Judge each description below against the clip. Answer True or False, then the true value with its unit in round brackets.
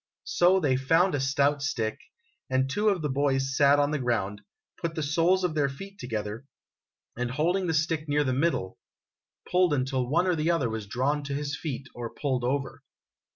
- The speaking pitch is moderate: True (145 Hz)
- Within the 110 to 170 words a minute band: False (195 wpm)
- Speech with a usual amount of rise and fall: True (3.9 semitones)